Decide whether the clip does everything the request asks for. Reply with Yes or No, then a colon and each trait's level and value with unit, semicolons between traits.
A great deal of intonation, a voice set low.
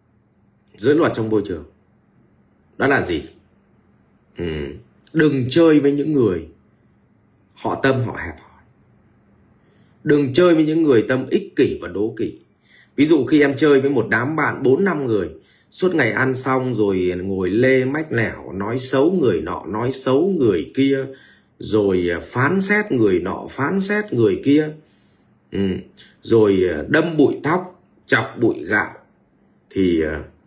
Yes: wide, 7.1 semitones; low, 130 Hz